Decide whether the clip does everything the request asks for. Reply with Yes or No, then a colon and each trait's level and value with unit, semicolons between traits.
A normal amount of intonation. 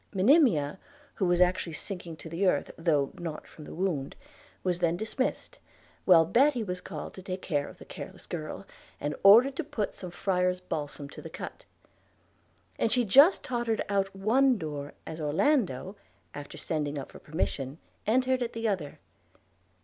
No: wide, 6.1 semitones